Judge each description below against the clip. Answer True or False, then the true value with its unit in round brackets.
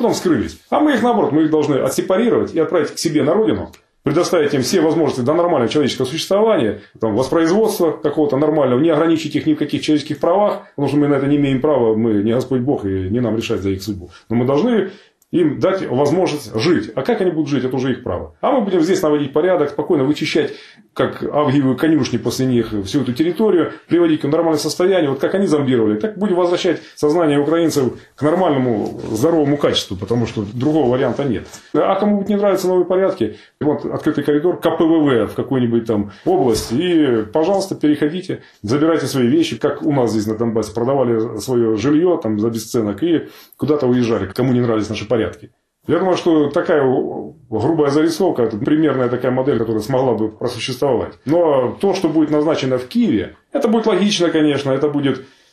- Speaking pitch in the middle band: True (145 Hz)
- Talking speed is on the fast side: True (190 wpm)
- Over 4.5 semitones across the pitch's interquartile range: True (5.6 semitones)